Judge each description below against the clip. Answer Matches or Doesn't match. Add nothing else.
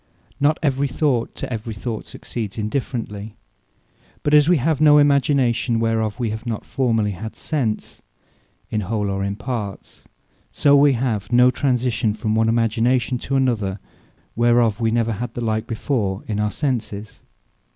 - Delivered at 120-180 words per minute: Matches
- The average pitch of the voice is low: Matches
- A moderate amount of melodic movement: Matches